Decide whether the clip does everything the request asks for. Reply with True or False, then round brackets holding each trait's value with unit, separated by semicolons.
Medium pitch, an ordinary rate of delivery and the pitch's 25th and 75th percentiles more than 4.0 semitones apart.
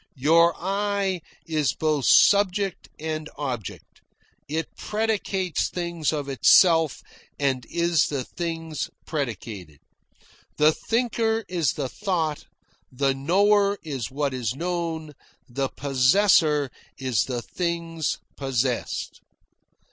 False (155 Hz; 100 wpm; 4.8 semitones)